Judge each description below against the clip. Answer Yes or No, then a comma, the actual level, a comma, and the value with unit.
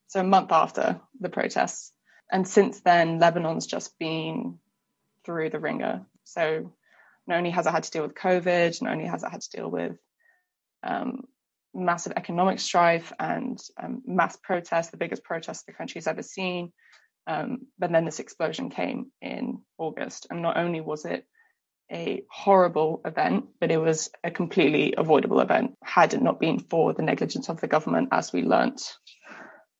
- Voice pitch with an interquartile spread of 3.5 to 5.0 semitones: Yes, average, 3.9 semitones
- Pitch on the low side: No, medium, 175 Hz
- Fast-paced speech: No, average, 170 wpm